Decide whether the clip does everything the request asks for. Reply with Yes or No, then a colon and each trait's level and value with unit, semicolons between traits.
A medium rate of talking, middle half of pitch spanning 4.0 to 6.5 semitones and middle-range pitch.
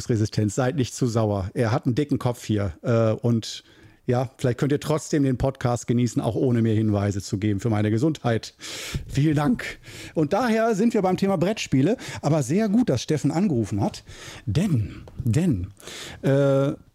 No: average, 170 wpm; wide, 5.5 semitones; low, 125 Hz